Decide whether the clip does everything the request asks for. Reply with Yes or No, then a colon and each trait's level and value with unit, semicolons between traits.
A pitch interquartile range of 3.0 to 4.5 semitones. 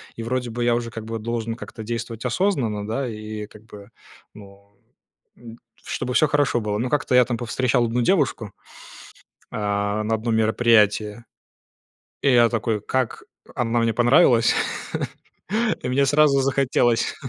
No: narrow, 2.5 semitones